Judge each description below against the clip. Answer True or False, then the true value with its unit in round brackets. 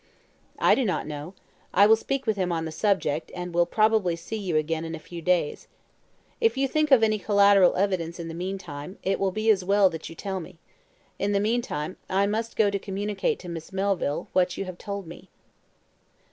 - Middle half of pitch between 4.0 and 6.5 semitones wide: False (3.4 semitones)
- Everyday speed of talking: False (215 wpm)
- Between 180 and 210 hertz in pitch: True (190 Hz)